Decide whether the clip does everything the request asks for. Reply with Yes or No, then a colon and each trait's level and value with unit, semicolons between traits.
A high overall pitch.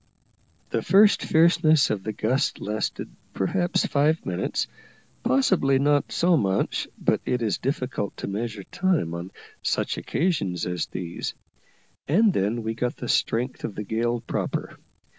No: low, 120 Hz